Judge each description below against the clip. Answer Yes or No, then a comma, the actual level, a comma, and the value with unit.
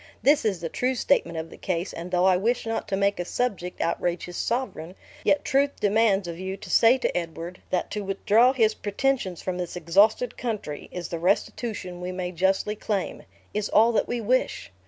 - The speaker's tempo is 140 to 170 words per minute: No, average, 200 wpm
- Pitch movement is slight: No, average, 4.2 semitones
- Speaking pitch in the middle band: No, high, 195 Hz